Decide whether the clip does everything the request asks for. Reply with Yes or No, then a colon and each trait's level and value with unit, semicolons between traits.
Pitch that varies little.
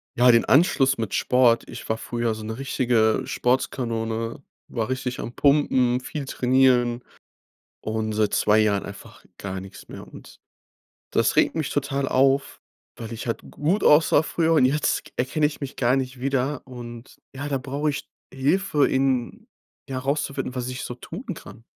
No: average, 3.1 semitones